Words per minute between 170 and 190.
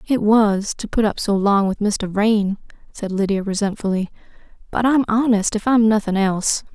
Yes: average, 180 wpm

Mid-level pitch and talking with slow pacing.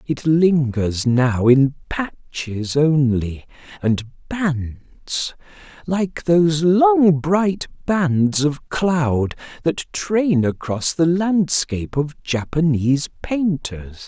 Yes: medium, 150 Hz; slow, 95 wpm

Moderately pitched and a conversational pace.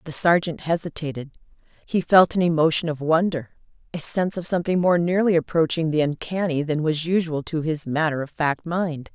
Yes: medium, 160 Hz; average, 170 wpm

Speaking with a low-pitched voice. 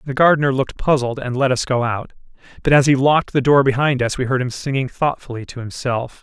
Yes: low, 130 Hz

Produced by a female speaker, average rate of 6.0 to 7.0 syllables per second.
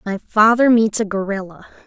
No: female; 5.1 syllables/s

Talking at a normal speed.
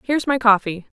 Yes: average, 180 wpm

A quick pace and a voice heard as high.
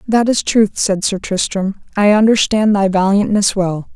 No: average, 165 wpm; high, 200 Hz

